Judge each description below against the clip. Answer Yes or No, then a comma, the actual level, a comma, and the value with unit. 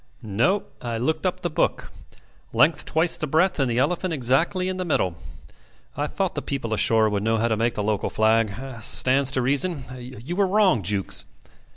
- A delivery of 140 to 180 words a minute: No, average, 190 wpm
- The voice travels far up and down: Yes, wide, 6.4 semitones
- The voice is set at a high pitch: No, low, 130 Hz